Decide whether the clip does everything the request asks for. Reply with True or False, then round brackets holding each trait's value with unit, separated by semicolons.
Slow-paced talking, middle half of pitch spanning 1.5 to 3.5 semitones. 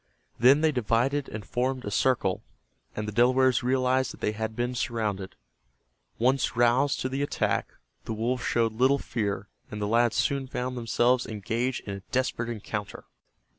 False (165 wpm; 2.8 semitones)